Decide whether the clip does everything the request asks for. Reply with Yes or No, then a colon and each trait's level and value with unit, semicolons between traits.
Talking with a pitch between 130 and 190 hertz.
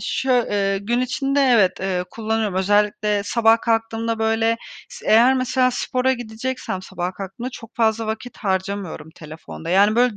No: high, 225 Hz